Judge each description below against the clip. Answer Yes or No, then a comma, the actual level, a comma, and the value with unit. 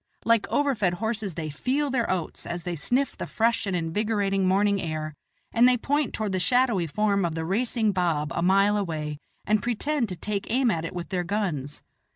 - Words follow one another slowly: No, average, 195 wpm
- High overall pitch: Yes, high, 200 Hz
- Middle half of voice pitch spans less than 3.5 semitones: No, average, 5.1 semitones